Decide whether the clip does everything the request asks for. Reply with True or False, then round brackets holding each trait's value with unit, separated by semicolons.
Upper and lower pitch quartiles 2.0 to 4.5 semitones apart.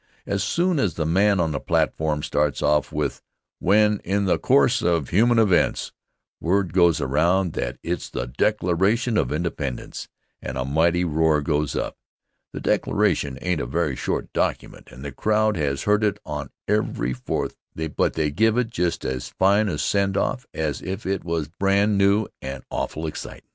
False (5.3 semitones)